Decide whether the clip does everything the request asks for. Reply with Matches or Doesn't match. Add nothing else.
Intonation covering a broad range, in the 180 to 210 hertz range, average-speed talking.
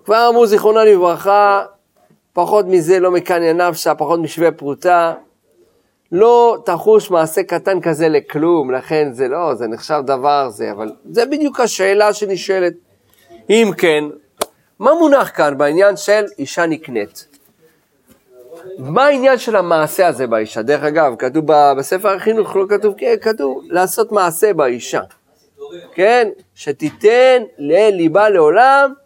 Matches